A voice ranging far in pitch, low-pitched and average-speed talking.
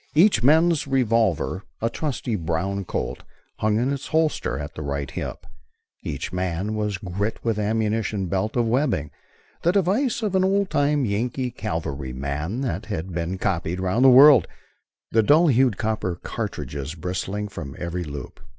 Yes: wide, 7.3 semitones; low, 105 Hz; average, 155 wpm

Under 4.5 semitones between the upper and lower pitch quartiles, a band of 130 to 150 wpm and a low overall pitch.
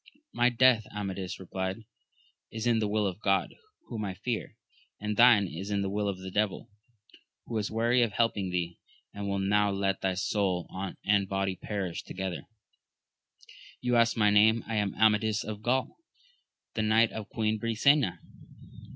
No: narrow, 2.5 semitones; average, 170 wpm; low, 105 Hz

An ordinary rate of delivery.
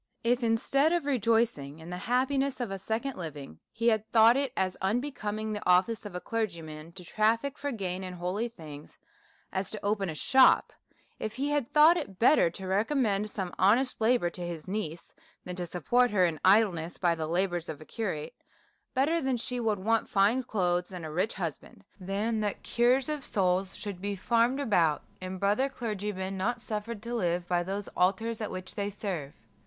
Yes: average, 190 wpm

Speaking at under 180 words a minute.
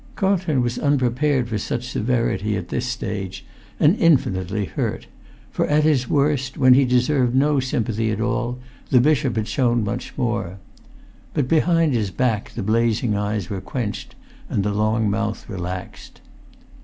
Yes: average, 155 wpm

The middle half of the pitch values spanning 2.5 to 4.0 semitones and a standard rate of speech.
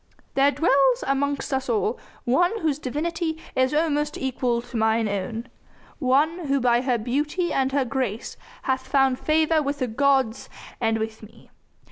Yes: average, 3.6 semitones; average, 155 wpm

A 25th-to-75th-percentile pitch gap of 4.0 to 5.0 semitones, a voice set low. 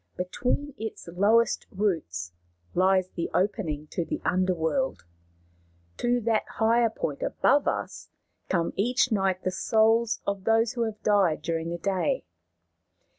No: average, 4.3 semitones; high, 200 Hz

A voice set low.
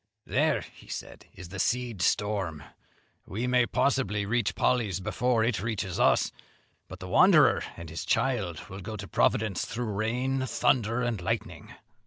Yes: low, 110 Hz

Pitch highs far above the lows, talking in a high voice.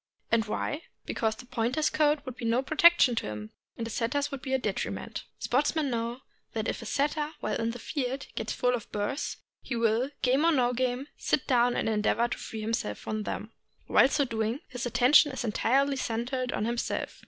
No: average, 3.3 semitones; high, 245 Hz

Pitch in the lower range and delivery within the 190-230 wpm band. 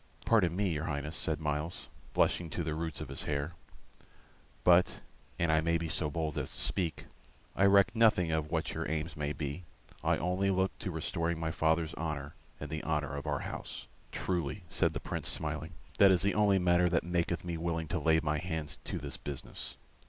Yes: very low, 80 Hz; average, 200 wpm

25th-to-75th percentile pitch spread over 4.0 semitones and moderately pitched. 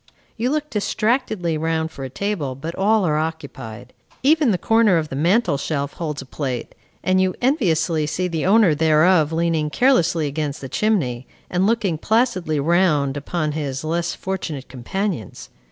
Yes: average, 4.8 semitones; medium, 165 Hz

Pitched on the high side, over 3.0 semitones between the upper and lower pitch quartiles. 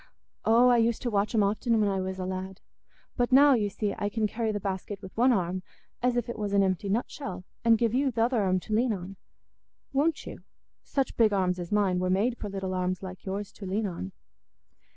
Yes: high, 205 Hz; average, 3.7 semitones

